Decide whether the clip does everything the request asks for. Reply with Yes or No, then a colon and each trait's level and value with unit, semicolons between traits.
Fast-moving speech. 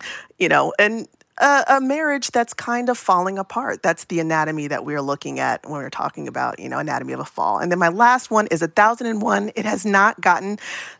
Yes: fast, 230 wpm